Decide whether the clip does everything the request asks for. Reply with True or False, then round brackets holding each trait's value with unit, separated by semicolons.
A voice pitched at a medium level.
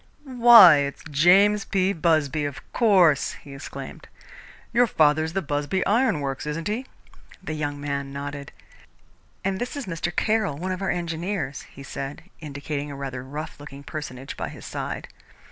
True (155 Hz)